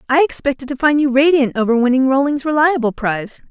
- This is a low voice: No, very high, 270 Hz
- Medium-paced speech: Yes, average, 190 wpm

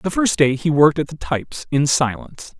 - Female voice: No, male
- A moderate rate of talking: No, fast, 230 wpm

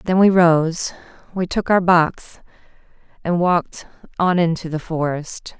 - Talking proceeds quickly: No, average, 140 wpm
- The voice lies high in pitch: No, medium, 170 Hz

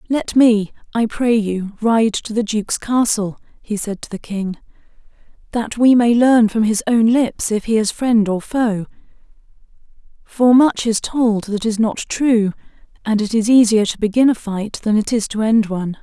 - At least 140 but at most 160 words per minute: No, average, 190 wpm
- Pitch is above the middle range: Yes, high, 220 Hz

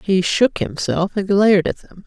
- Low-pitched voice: No, high, 190 Hz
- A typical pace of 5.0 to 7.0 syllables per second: No, 4.6 syllables/s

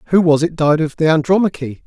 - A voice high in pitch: No, medium, 160 Hz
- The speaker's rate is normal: No, fast, 225 wpm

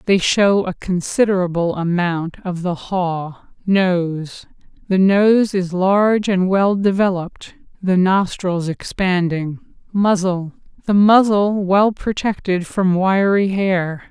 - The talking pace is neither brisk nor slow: No, slow, 105 wpm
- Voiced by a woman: Yes, female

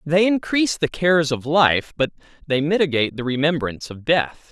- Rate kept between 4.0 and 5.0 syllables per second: No, 5.5 syllables/s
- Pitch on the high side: No, medium, 150 Hz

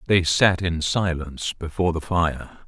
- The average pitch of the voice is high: No, very low, 85 Hz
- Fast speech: No, average, 155 wpm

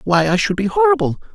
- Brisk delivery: Yes, fast, 225 wpm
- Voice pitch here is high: No, medium, 170 Hz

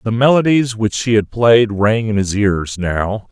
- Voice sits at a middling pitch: No, low, 110 Hz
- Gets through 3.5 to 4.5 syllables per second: Yes, 4.1 syllables/s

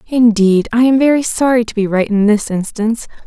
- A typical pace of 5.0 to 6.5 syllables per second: Yes, 5.5 syllables/s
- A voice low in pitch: No, high, 225 Hz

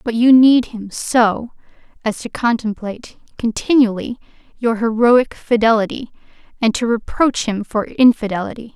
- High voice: Yes, high, 230 Hz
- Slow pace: Yes, slow, 125 wpm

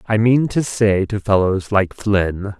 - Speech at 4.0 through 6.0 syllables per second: No, 3.7 syllables/s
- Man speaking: Yes, male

